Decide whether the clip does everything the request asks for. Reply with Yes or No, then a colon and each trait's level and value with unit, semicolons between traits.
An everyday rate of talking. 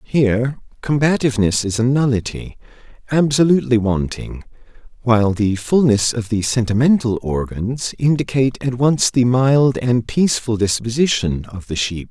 No: slow, 115 wpm